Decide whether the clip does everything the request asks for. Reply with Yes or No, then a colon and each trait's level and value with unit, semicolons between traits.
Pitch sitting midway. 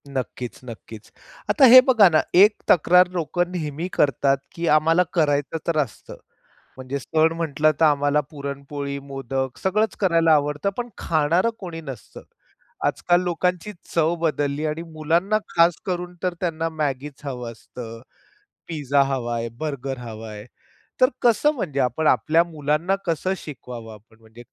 Yes: medium, 150 Hz